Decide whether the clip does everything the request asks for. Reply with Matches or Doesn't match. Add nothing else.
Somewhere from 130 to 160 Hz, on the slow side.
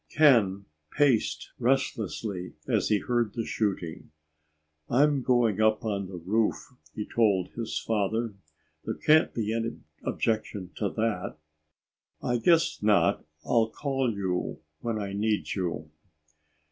Doesn't match